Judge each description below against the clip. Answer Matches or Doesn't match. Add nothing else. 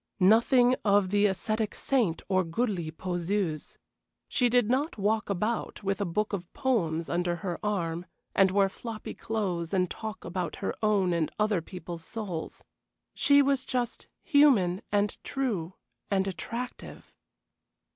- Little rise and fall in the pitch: Doesn't match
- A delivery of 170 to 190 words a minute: Doesn't match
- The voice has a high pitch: Matches